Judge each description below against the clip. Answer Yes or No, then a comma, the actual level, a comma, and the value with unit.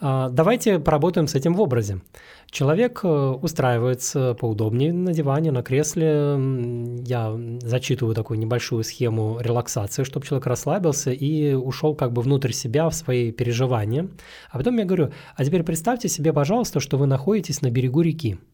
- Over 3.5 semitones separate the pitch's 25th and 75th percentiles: Yes, average, 4.5 semitones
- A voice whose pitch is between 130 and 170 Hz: Yes, low, 135 Hz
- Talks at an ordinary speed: Yes, average, 150 wpm